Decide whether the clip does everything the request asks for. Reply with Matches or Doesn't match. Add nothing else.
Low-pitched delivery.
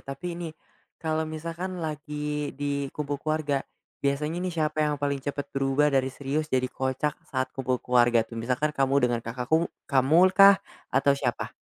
Doesn't match